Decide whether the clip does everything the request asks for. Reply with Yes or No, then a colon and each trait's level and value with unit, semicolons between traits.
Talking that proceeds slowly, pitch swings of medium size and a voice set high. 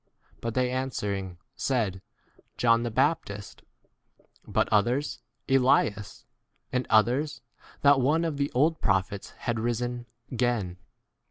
No: slow, 120 wpm; average, 4.0 semitones; low, 120 Hz